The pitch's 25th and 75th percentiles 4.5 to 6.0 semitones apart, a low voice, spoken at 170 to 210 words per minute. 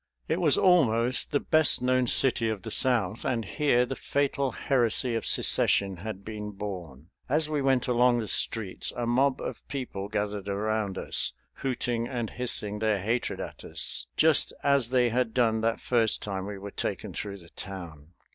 No: average, 3.7 semitones; low, 115 Hz; average, 175 wpm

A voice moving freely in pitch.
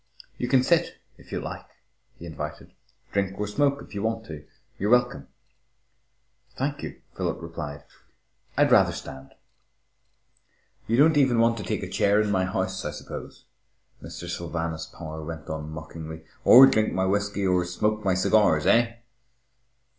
Yes: wide, 5.9 semitones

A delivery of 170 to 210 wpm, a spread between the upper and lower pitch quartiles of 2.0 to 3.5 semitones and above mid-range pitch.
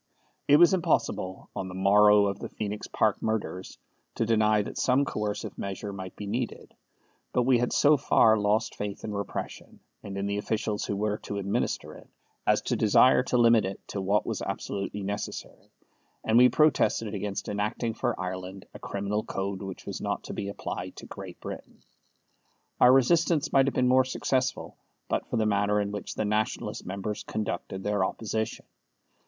No: average, 180 wpm; average, 2.8 semitones; low, 105 Hz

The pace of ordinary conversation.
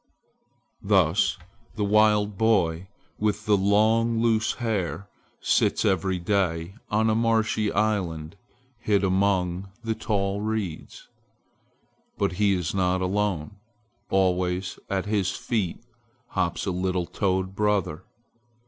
No: slow, 110 wpm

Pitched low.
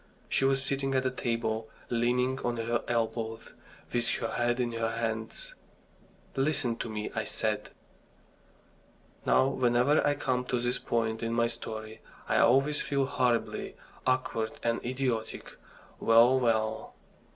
Yes: low, 120 Hz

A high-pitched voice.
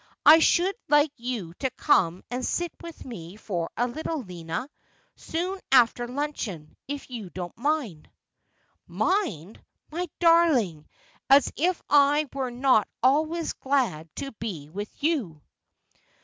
Yes: very high, 255 Hz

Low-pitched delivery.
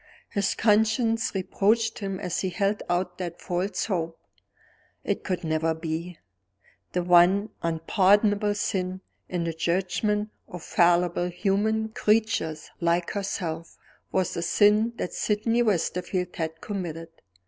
No: medium, 185 Hz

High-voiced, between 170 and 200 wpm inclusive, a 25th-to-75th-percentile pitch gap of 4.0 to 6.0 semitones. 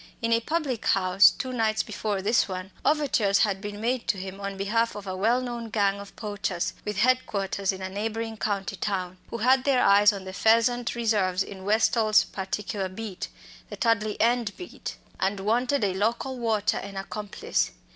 No: high, 210 Hz; average, 185 wpm; average, 2.9 semitones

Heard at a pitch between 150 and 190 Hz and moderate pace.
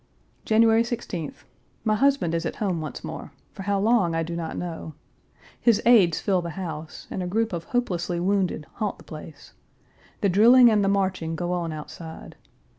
Yes: medium, 185 Hz; average, 180 wpm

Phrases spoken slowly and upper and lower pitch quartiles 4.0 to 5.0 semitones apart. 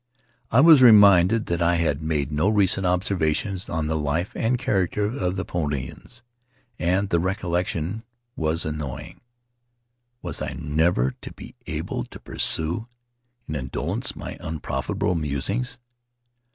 Yes: slow, 130 wpm; average, 4.4 semitones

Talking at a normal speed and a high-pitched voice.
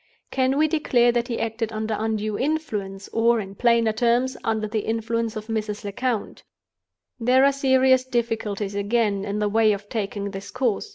Yes: average, 170 wpm; high, 225 Hz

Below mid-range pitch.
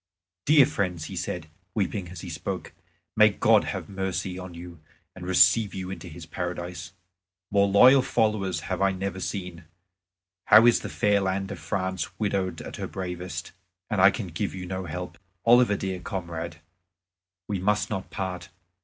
Yes: very low, 95 Hz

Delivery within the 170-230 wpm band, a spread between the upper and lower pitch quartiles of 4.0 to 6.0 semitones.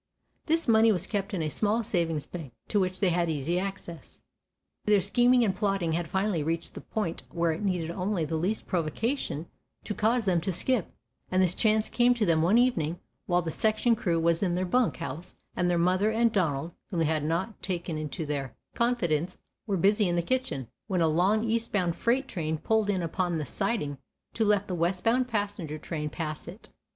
Yes: average, 200 wpm; average, 4.5 semitones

